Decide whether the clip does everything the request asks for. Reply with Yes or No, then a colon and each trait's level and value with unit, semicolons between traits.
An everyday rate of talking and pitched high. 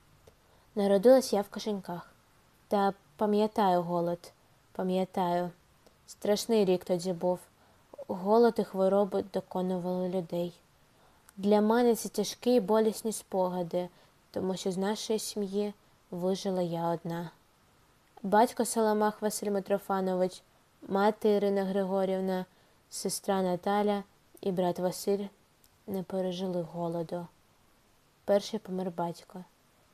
No: slow, 100 wpm; high, 195 Hz